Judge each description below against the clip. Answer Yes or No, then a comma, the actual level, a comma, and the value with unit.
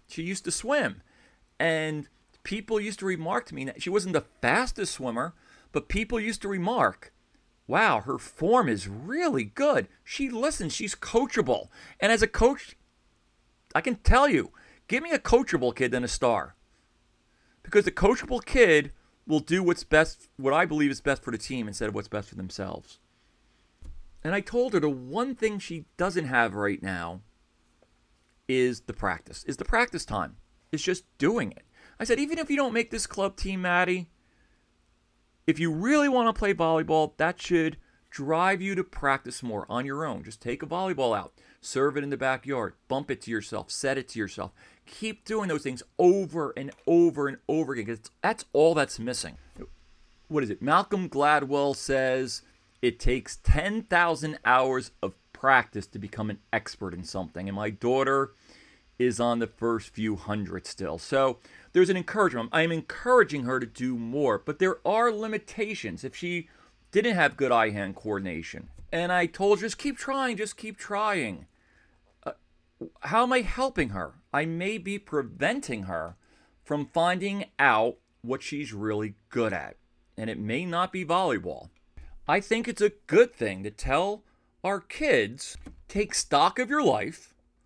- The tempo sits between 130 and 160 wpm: No, average, 175 wpm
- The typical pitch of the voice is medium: Yes, medium, 155 Hz